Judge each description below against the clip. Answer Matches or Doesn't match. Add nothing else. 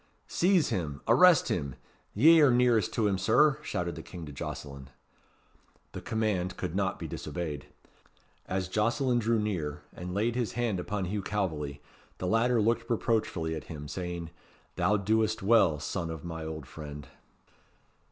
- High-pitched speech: Doesn't match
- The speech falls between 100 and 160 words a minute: Matches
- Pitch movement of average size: Doesn't match